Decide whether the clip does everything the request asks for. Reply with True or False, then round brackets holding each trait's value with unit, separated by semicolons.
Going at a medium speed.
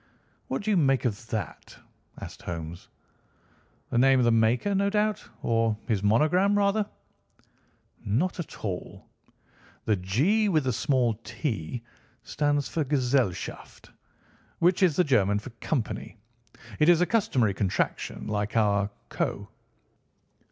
False (130 wpm)